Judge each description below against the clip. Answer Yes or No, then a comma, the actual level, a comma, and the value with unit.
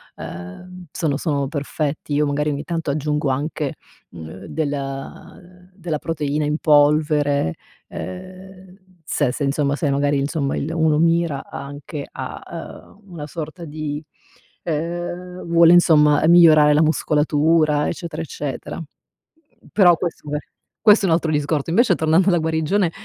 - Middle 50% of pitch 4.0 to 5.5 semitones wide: No, narrow, 2.6 semitones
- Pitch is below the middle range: No, medium, 155 Hz